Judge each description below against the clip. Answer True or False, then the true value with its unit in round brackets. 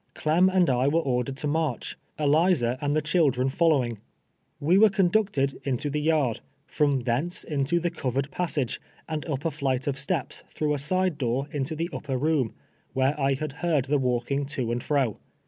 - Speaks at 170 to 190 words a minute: True (185 wpm)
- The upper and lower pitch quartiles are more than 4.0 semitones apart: False (3.3 semitones)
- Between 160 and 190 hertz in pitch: False (145 Hz)